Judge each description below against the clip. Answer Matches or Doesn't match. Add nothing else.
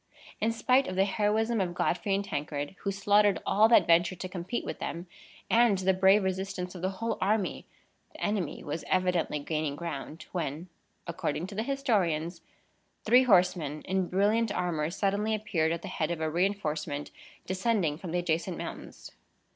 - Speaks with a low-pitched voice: Doesn't match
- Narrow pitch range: Doesn't match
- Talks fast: Doesn't match